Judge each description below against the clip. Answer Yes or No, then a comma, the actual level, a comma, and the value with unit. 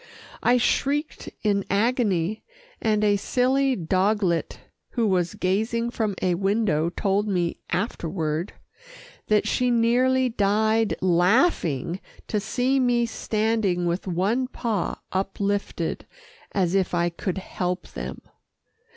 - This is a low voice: No, high, 205 Hz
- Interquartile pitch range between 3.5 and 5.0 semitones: Yes, average, 4.3 semitones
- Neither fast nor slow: No, slow, 115 wpm